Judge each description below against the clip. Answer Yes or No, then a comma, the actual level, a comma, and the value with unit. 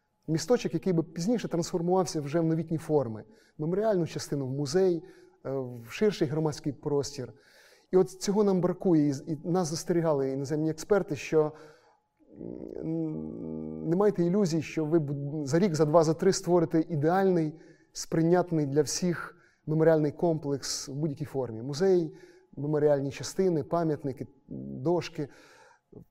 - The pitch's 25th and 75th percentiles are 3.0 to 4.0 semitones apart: Yes, average, 3.6 semitones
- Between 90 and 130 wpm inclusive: Yes, average, 125 wpm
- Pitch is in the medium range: Yes, medium, 160 Hz